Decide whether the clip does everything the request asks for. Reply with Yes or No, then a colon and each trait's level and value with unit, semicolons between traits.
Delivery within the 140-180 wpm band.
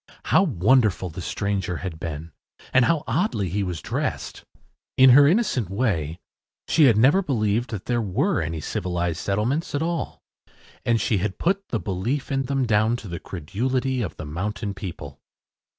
Yes: average, 165 wpm